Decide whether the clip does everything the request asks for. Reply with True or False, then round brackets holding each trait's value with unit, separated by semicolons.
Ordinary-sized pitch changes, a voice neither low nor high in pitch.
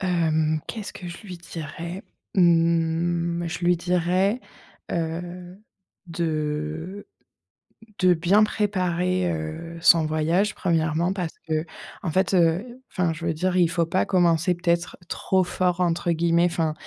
False (1.8 semitones; 170 Hz)